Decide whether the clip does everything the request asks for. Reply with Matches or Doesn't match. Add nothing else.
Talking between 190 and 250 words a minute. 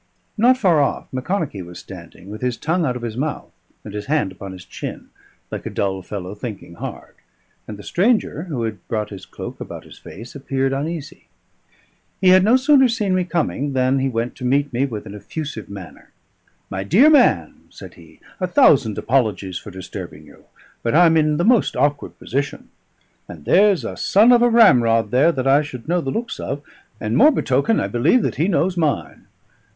Matches